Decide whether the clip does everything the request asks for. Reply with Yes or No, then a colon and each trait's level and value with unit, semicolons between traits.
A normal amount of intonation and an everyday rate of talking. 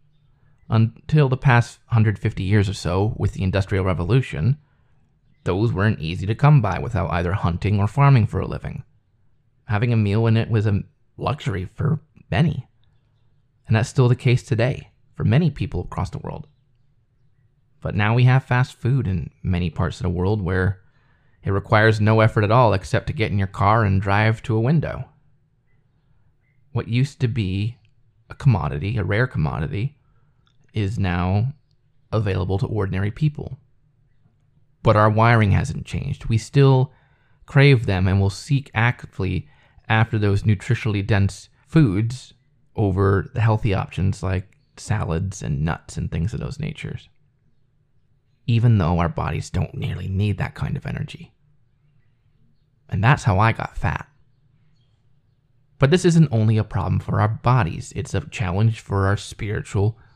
Yes: average, 4.7 semitones; average, 155 wpm